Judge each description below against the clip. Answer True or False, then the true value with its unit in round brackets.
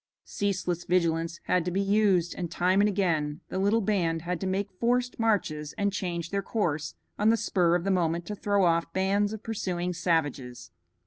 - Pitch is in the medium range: True (180 Hz)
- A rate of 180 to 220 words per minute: True (190 wpm)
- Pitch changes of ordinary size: True (3.2 semitones)